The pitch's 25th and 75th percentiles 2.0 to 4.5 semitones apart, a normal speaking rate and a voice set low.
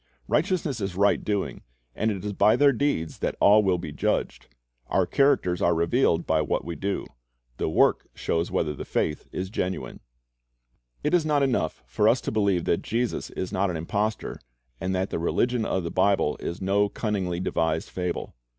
Yes: average, 4.0 semitones; average, 185 wpm; very low, 95 Hz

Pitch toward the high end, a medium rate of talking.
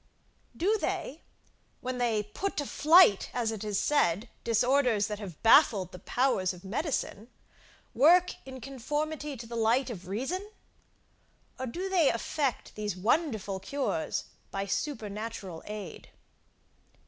No: high, 235 Hz; slow, 130 wpm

